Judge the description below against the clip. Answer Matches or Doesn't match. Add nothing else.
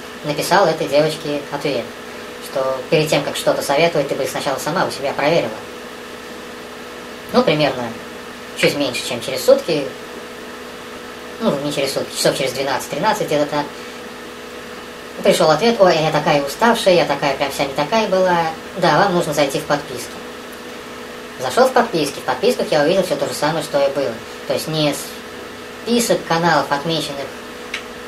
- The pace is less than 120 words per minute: Doesn't match